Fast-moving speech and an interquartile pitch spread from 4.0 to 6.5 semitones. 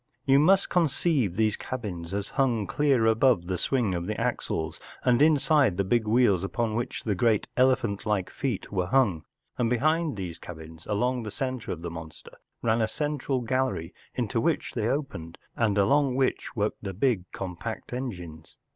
No: average, 175 wpm; wide, 5.6 semitones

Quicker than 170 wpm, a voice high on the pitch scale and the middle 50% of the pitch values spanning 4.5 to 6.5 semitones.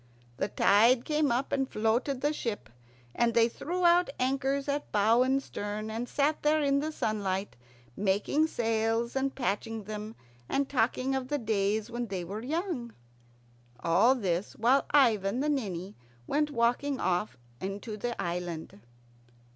No: average, 150 wpm; high, 235 Hz; average, 4.9 semitones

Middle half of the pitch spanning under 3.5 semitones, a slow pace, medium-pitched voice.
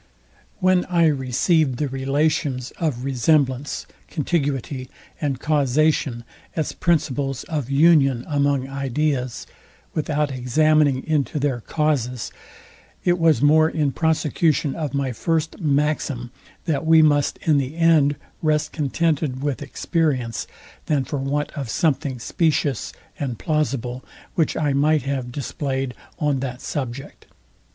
Yes: average, 2.8 semitones; slow, 120 wpm; medium, 145 Hz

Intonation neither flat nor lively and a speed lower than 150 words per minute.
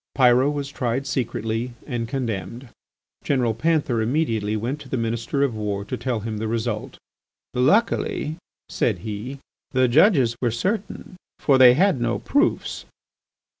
Yes: average, 3.7 semitones; average, 140 wpm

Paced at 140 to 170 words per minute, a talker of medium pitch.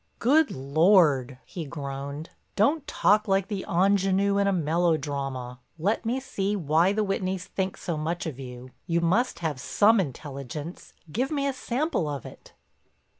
Yes: average, 150 wpm; medium, 175 Hz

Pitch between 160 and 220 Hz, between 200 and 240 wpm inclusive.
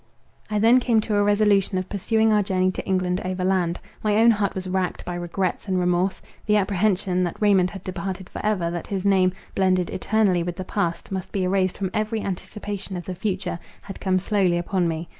Yes: high, 190 Hz; fast, 205 wpm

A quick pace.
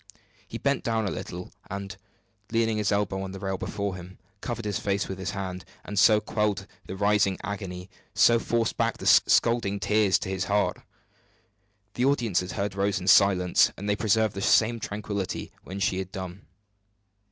No: average, 180 wpm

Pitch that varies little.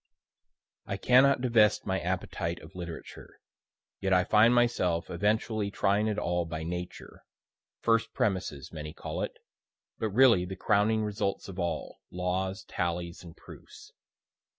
No: average, 3.7 semitones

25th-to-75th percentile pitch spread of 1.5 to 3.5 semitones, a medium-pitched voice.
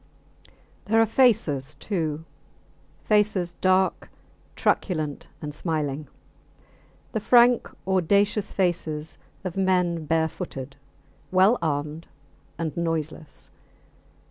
No: average, 4.4 semitones; medium, 170 Hz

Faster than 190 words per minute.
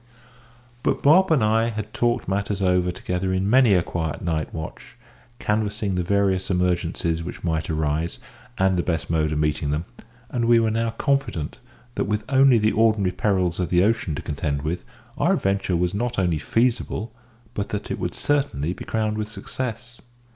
No: average, 180 wpm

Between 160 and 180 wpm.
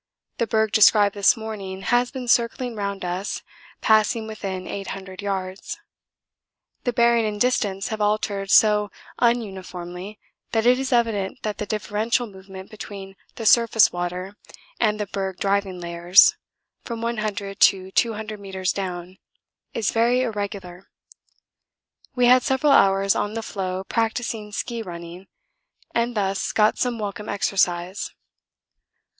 No: slow, 135 wpm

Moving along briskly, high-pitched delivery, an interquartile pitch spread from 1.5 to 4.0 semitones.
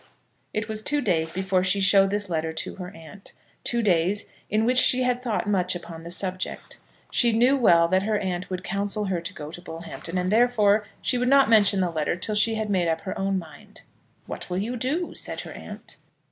Yes: fast, 215 wpm; high, 195 Hz; average, 3.7 semitones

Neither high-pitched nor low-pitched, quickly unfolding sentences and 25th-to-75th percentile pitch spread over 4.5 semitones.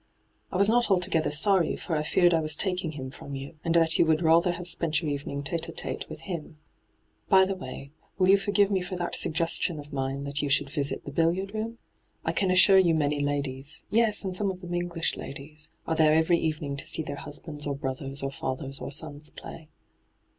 No: medium, 160 Hz; fast, 225 wpm; average, 4.0 semitones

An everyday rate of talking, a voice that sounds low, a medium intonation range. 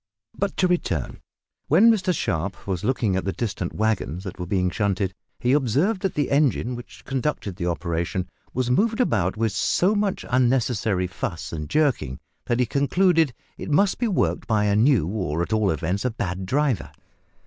No: average, 180 wpm; low, 110 Hz; wide, 7.9 semitones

